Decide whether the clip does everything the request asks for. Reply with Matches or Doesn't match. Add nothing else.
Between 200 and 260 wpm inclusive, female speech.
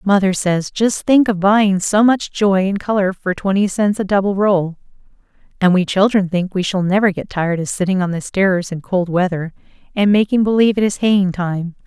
Matches